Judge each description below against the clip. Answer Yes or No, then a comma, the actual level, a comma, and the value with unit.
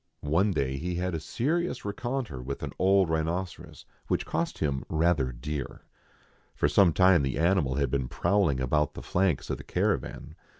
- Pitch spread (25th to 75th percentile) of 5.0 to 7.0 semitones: Yes, wide, 5.6 semitones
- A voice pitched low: Yes, very low, 80 Hz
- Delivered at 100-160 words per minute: No, average, 180 wpm